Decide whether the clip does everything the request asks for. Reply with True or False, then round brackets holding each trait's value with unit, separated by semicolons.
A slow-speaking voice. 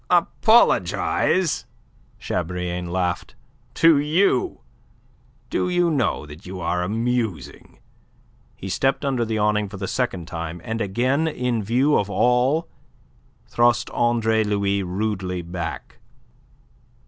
True (110 wpm)